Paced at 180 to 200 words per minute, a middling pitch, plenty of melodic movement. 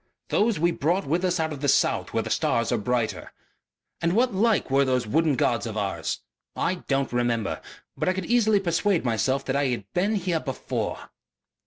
Yes: average, 195 wpm; medium, 150 Hz; wide, 7.0 semitones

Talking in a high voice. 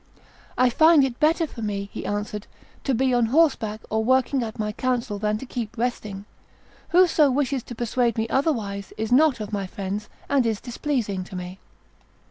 Yes: high, 235 Hz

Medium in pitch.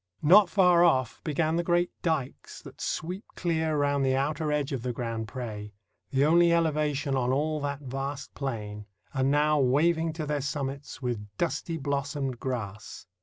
Yes: medium, 145 Hz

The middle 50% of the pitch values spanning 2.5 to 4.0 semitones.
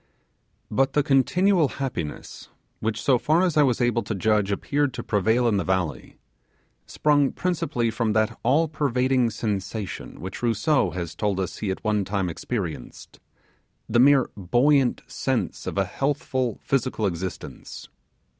No: average, 5.3 semitones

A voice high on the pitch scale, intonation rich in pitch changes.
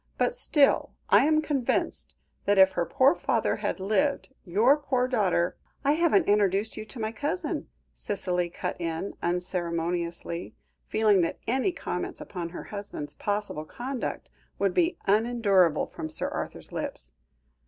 Yes: high, 205 Hz; wide, 6.7 semitones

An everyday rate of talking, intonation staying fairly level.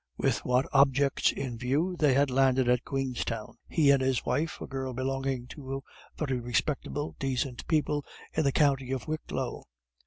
Yes: average, 155 wpm; narrow, 1.9 semitones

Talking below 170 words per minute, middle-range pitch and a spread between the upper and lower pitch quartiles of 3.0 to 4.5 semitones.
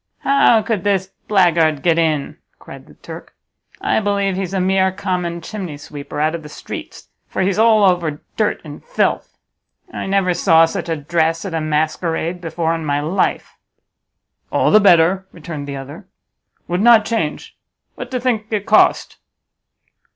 Yes: average, 160 wpm; medium, 175 Hz; average, 3.8 semitones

